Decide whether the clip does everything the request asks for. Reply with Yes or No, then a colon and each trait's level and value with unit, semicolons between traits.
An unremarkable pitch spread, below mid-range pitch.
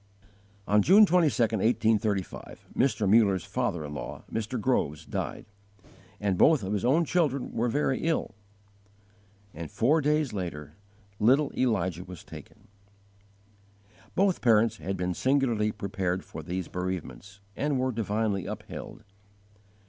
No: wide, 5.9 semitones; low, 110 Hz